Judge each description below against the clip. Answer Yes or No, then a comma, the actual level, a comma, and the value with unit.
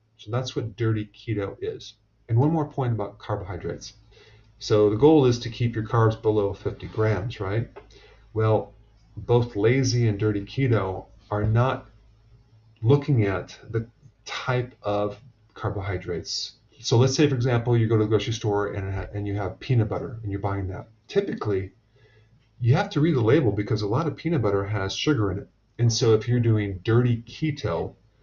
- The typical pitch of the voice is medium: No, low, 110 Hz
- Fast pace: No, average, 180 wpm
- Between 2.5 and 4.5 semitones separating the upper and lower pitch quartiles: Yes, average, 3.0 semitones